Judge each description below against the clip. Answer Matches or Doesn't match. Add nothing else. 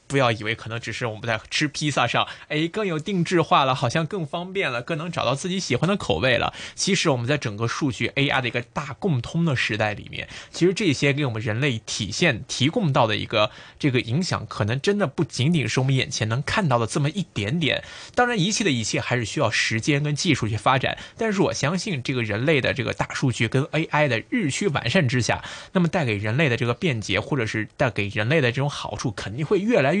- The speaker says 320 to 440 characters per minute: Matches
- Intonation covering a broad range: Matches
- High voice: Doesn't match